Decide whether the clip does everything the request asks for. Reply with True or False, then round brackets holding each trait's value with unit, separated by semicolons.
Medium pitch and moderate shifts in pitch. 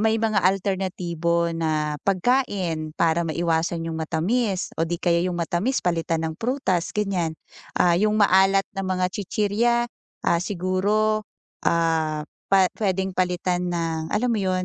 True (180 Hz; 3.2 semitones)